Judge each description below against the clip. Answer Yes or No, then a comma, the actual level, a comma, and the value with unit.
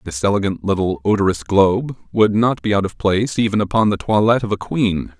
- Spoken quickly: Yes, fast, 210 wpm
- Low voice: Yes, low, 100 Hz